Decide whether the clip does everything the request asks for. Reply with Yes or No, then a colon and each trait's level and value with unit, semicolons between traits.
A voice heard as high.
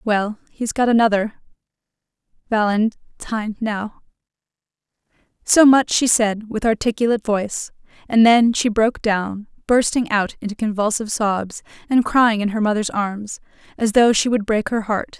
Yes: high, 215 Hz